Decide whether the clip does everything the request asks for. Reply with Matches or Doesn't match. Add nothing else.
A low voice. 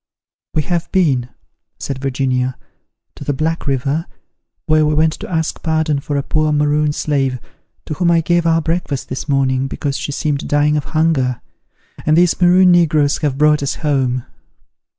Doesn't match